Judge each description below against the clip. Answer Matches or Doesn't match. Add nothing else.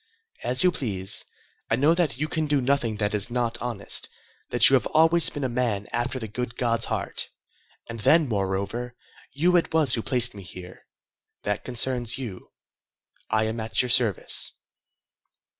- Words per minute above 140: Matches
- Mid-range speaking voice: Doesn't match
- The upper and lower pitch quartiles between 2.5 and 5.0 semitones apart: Matches